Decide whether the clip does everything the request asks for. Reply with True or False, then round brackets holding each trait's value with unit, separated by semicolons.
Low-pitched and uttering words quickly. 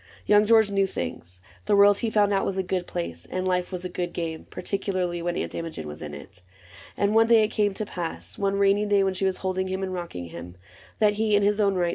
False (190 Hz; 270 wpm)